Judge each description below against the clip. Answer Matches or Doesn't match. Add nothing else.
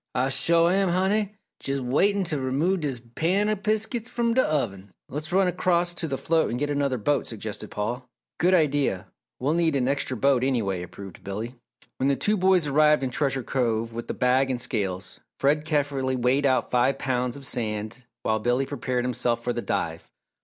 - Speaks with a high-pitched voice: Doesn't match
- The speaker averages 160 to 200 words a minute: Matches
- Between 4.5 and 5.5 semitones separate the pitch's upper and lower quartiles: Matches